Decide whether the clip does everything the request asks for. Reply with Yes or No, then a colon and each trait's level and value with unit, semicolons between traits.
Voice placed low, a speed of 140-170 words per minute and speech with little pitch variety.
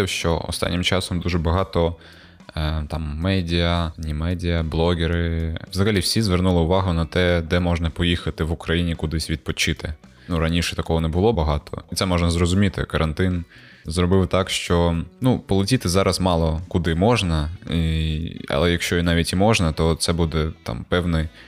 Yes: very low, 85 Hz; fast, 155 wpm; narrow, 2.0 semitones